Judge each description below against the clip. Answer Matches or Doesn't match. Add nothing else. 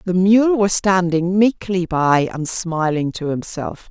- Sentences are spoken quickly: Doesn't match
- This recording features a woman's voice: Matches